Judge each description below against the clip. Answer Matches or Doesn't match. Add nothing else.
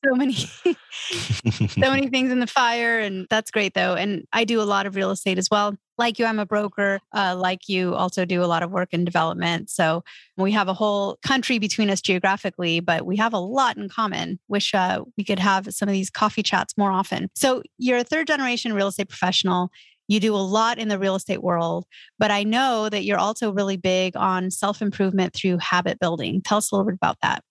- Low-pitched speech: Doesn't match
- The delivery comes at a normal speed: Doesn't match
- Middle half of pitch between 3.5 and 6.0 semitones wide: Doesn't match